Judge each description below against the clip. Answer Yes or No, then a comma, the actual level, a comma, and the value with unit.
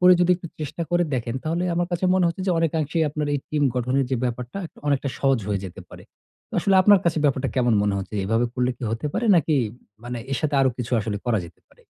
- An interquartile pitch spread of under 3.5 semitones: No, wide, 5.5 semitones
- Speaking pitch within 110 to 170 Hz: Yes, medium, 140 Hz